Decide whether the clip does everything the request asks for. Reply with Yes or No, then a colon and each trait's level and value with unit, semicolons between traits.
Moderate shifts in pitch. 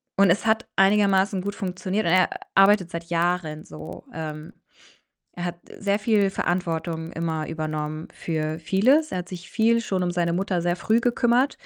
Yes: average, 3.4 semitones